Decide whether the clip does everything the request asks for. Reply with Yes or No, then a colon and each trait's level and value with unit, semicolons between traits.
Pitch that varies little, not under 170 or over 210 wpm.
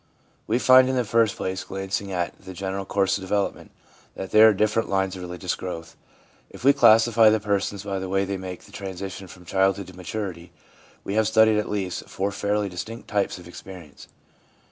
Yes: narrow, 2.3 semitones; average, 195 wpm